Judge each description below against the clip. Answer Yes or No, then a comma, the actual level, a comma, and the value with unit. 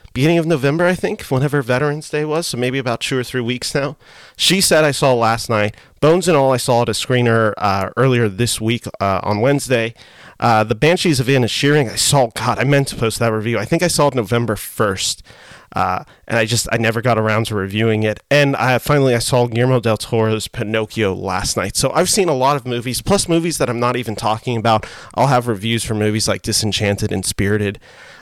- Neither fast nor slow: No, fast, 230 wpm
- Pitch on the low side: Yes, low, 120 Hz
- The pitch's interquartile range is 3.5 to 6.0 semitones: Yes, average, 4.0 semitones